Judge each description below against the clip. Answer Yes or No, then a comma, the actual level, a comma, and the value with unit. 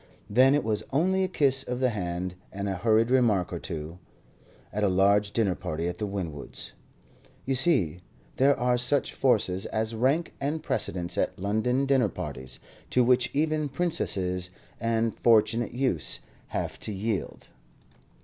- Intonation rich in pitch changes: Yes, wide, 5.8 semitones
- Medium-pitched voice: No, low, 115 Hz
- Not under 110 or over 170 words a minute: Yes, average, 155 wpm